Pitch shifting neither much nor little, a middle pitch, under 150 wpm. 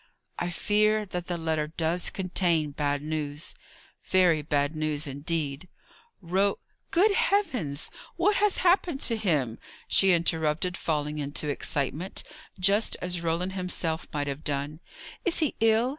Yes: average, 4.7 semitones; medium, 170 Hz; average, 140 wpm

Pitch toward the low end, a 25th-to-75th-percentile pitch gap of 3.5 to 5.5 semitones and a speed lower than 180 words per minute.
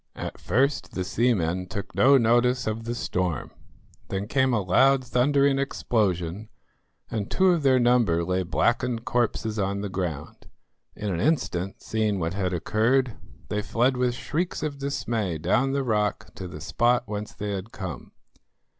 Yes: low, 110 Hz; average, 5.2 semitones; average, 160 wpm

